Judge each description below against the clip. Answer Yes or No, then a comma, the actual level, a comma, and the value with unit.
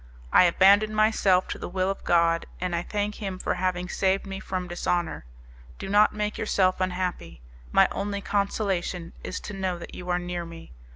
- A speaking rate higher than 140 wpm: Yes, average, 185 wpm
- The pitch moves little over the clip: Yes, narrow, 2.2 semitones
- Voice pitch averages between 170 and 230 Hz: Yes, medium, 185 Hz